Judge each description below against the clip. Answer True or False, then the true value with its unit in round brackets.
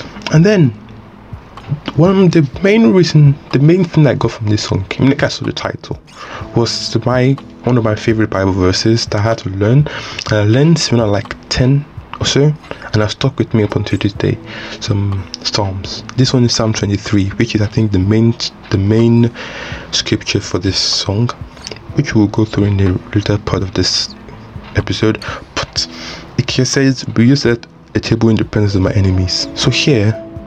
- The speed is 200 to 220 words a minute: True (205 wpm)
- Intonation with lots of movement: False (3.8 semitones)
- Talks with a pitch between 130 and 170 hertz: False (110 Hz)